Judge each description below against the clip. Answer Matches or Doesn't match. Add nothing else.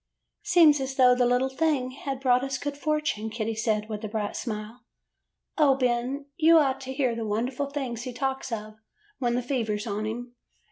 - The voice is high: Matches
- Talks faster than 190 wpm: Matches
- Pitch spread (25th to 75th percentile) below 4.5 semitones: Matches